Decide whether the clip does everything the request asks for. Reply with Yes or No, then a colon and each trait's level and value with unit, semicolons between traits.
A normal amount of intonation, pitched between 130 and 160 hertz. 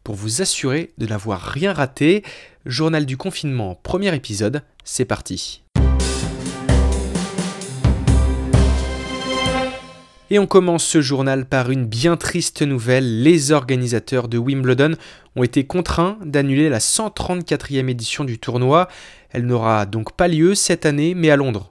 No: wide, 6.5 semitones; low, 135 Hz